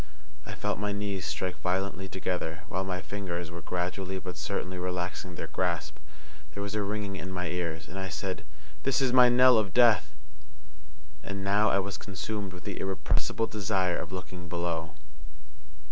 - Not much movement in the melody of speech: Yes, narrow, 2.2 semitones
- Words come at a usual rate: Yes, average, 170 wpm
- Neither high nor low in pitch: No, very low, 95 Hz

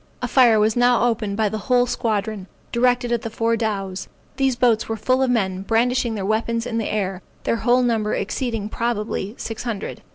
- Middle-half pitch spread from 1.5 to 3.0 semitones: Yes, narrow, 2.4 semitones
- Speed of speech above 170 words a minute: Yes, average, 195 wpm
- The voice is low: No, high, 225 Hz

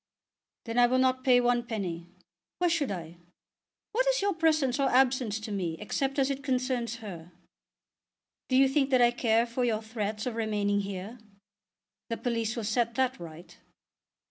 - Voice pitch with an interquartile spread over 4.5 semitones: No, average, 3.7 semitones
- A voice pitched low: No, high, 240 Hz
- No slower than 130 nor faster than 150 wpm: No, average, 170 wpm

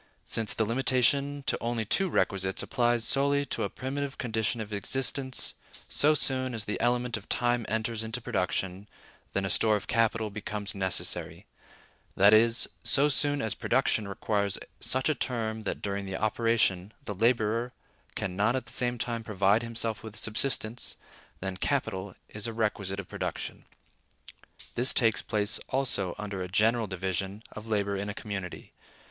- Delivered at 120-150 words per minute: No, average, 160 wpm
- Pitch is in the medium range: No, low, 110 Hz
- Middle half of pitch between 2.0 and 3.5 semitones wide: Yes, average, 3.2 semitones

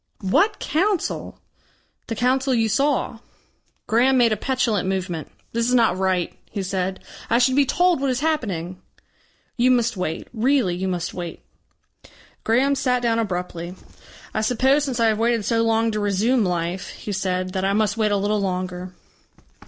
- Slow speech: No, average, 170 wpm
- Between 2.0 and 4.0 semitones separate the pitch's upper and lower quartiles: No, average, 5.1 semitones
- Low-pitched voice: No, high, 220 Hz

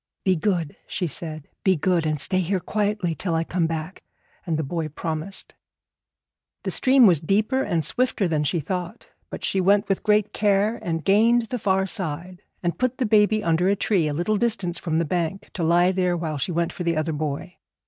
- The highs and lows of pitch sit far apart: No, average, 3.9 semitones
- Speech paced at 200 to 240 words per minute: Yes, fast, 205 wpm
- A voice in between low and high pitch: Yes, medium, 180 Hz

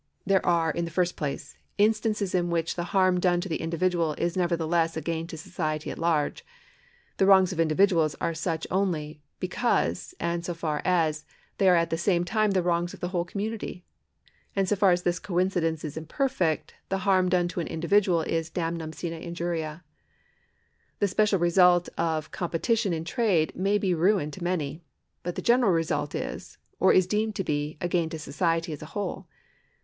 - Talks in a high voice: No, medium, 175 Hz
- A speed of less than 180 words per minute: No, average, 195 wpm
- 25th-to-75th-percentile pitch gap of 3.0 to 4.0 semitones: No, narrow, 2.4 semitones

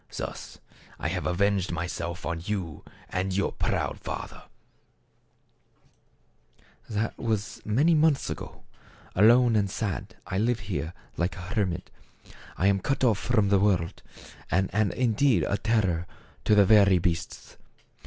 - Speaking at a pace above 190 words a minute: No, average, 140 wpm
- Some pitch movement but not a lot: Yes, average, 3.5 semitones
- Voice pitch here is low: Yes, low, 100 Hz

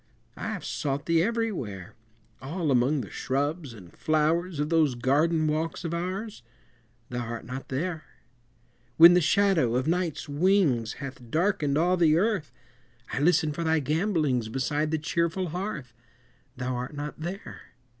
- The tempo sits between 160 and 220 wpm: No, average, 150 wpm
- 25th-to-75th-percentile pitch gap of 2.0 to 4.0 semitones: No, average, 4.5 semitones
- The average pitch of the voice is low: No, medium, 155 Hz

